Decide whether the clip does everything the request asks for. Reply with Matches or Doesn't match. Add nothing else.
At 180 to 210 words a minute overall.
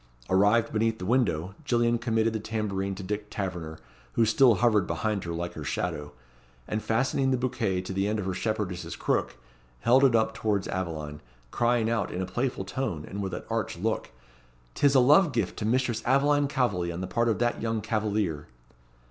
Matches